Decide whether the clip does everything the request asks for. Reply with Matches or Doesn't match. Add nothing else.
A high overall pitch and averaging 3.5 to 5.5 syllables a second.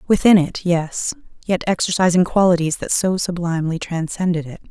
Doesn't match